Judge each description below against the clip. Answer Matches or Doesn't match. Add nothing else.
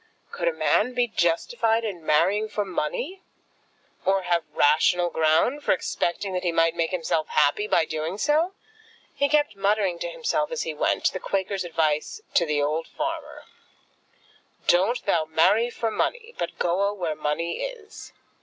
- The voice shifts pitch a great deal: Matches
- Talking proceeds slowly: Doesn't match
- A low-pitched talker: Doesn't match